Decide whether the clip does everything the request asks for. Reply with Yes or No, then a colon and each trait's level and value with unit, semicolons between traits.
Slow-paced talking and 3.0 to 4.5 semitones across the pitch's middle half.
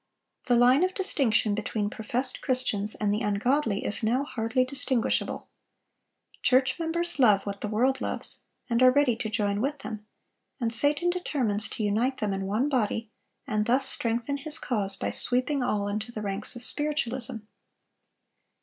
No: average, 160 wpm; average, 4.1 semitones